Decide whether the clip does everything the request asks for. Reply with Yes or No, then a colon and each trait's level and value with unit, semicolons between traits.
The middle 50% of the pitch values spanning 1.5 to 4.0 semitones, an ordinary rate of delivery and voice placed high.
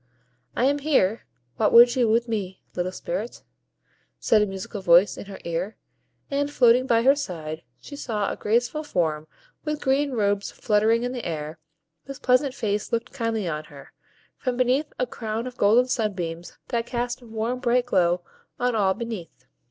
No: average, 4.8 semitones; average, 175 wpm; high, 230 Hz